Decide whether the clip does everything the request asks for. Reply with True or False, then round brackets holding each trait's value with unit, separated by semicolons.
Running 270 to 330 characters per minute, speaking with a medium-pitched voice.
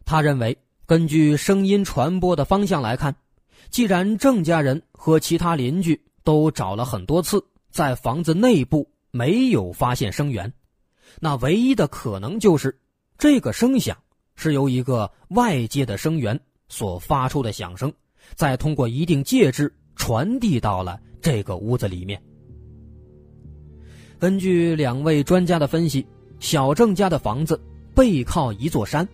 False (215 characters per minute; 150 Hz)